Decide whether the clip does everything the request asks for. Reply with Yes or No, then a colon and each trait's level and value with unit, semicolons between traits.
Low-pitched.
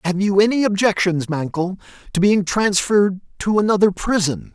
No: high, 195 Hz